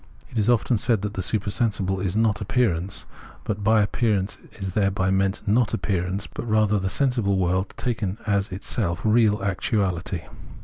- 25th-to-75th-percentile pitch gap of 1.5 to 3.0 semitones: Yes, narrow, 2.5 semitones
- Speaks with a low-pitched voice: Yes, low, 100 Hz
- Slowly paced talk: No, average, 160 wpm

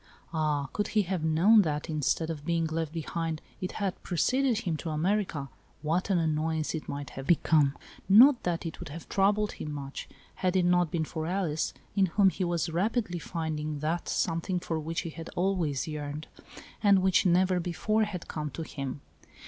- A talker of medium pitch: Yes, medium, 165 Hz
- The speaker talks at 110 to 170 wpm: No, average, 185 wpm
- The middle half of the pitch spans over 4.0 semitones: No, average, 3.4 semitones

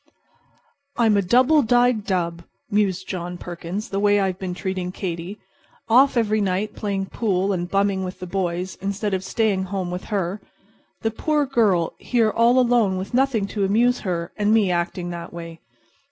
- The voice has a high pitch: Yes, high, 195 Hz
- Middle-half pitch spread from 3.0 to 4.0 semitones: Yes, average, 3.4 semitones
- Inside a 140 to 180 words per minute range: Yes, average, 170 wpm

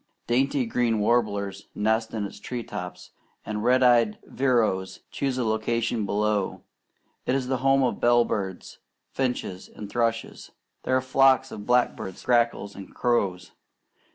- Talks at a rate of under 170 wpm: Yes, average, 145 wpm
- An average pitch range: Yes, average, 3.3 semitones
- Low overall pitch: Yes, low, 115 Hz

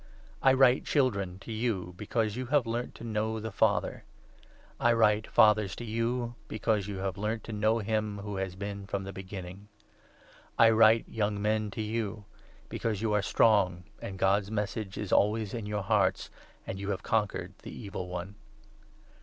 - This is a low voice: Yes, low, 105 Hz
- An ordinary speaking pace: Yes, average, 180 wpm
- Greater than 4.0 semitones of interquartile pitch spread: No, narrow, 2.4 semitones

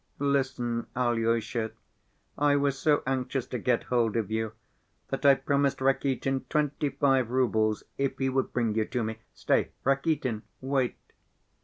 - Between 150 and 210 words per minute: No, average, 140 wpm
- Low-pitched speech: Yes, low, 130 Hz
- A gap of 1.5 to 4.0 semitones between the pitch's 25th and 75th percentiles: Yes, average, 3.0 semitones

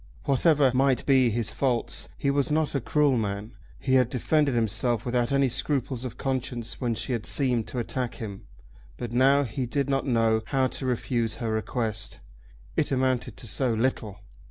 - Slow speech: No, average, 180 wpm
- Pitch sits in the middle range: No, low, 125 Hz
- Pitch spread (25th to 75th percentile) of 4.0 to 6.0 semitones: No, average, 2.9 semitones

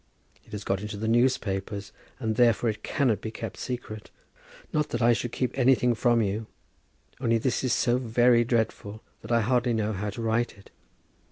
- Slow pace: No, average, 185 wpm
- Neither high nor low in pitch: No, low, 115 Hz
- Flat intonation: Yes, narrow, 2.3 semitones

